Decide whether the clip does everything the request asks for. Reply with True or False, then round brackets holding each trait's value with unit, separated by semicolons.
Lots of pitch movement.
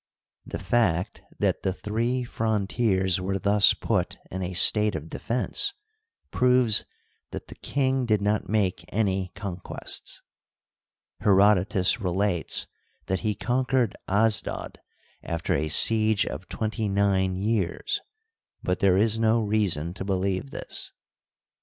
False (3.1 semitones)